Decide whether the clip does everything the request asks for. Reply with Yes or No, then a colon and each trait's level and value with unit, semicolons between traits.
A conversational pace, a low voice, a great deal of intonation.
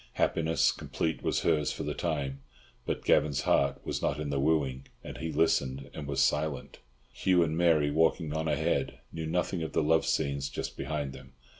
No: average, 185 wpm; very low, 75 Hz; narrow, 2.5 semitones